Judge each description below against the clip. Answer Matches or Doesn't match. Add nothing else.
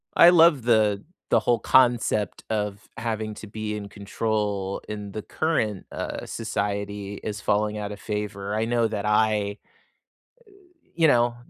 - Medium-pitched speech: Doesn't match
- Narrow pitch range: Matches